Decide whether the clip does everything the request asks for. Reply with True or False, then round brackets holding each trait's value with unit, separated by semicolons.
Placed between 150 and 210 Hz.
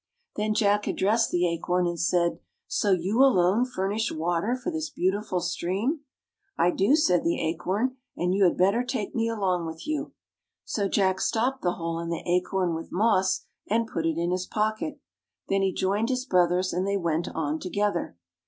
True (190 Hz)